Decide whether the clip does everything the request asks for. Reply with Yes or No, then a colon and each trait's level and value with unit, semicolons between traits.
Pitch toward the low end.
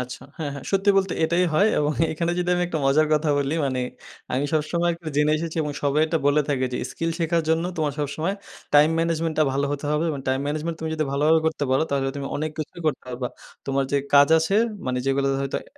No: medium, 150 Hz